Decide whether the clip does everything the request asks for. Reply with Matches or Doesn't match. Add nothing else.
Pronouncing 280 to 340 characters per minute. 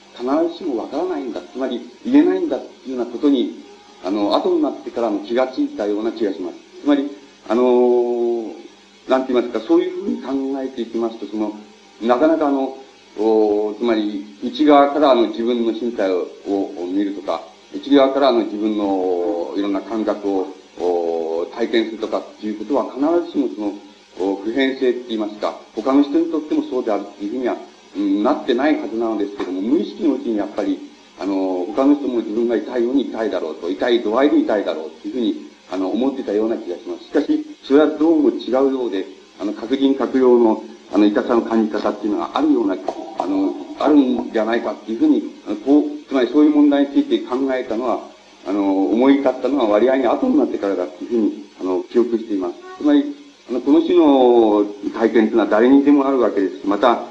Doesn't match